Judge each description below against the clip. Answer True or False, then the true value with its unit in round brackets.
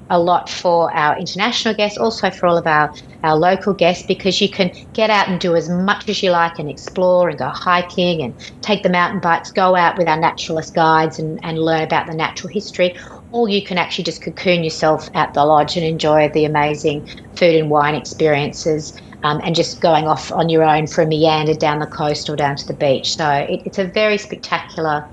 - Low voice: False (165 Hz)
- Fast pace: True (220 wpm)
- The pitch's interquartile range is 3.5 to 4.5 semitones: False (2.9 semitones)